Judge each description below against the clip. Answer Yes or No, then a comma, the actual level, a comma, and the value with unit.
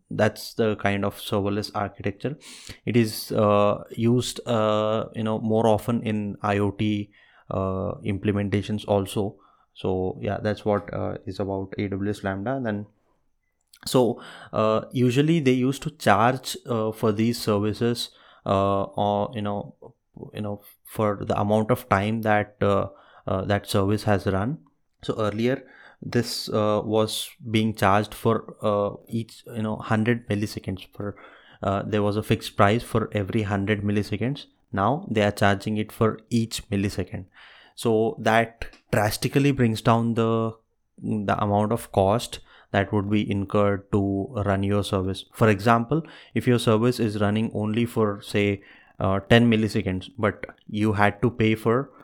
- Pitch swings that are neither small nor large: No, narrow, 2.1 semitones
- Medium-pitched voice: No, low, 105 Hz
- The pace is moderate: Yes, average, 150 wpm